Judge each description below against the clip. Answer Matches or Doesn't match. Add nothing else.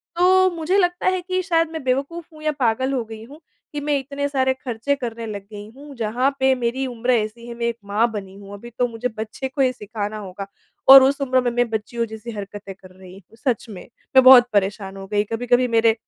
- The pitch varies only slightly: Doesn't match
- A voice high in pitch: Matches